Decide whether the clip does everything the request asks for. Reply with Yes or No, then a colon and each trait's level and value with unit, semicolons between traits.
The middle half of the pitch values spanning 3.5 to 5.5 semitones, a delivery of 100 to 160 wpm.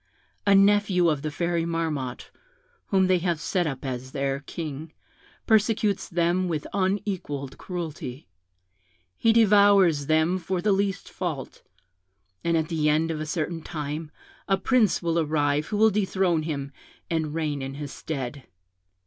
Yes: average, 4.2 semitones; average, 150 wpm